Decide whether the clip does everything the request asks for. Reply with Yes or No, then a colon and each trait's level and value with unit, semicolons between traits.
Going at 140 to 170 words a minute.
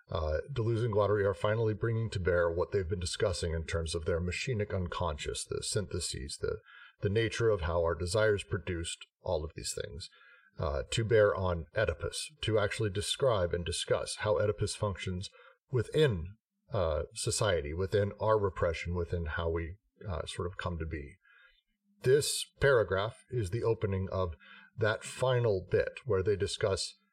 Yes: average, 160 wpm